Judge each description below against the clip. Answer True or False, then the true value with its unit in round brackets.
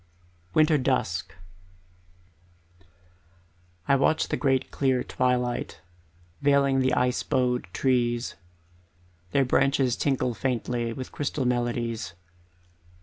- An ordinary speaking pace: False (90 wpm)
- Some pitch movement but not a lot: False (2.1 semitones)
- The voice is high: False (125 Hz)